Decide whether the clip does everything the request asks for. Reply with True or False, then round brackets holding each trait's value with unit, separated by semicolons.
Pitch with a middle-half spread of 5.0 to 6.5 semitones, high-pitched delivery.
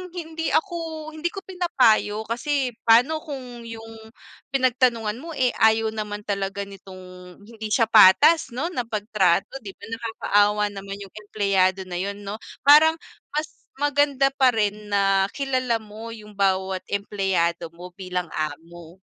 True (5.4 semitones; 220 Hz)